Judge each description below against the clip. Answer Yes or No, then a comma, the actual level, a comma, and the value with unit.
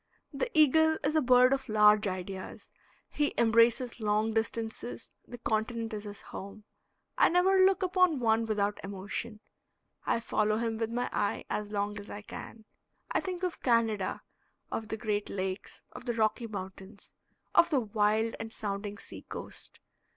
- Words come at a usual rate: Yes, average, 160 wpm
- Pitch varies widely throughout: No, average, 3.0 semitones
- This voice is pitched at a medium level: No, high, 220 Hz